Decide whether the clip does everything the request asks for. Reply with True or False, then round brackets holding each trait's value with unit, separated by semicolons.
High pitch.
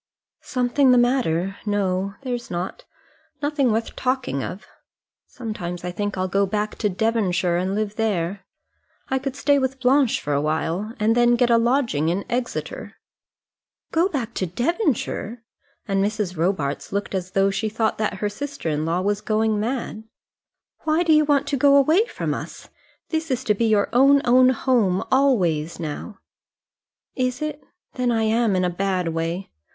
True (220 Hz)